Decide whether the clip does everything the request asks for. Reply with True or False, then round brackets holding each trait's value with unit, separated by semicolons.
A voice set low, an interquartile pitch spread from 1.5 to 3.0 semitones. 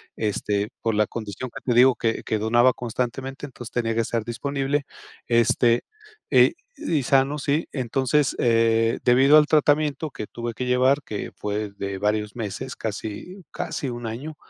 False (120 Hz; 3.4 semitones)